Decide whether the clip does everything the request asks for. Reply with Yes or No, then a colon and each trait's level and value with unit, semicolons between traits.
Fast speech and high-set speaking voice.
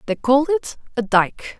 No: average, 190 wpm; very high, 255 Hz